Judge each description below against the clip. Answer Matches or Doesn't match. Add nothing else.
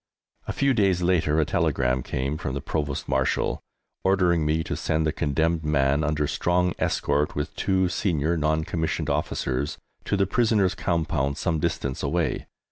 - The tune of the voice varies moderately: Matches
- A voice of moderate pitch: Doesn't match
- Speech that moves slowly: Doesn't match